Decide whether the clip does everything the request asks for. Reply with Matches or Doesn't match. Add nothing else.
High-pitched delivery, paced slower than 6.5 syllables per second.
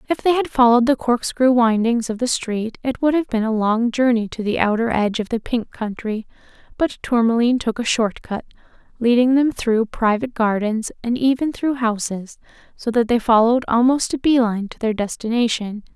Matches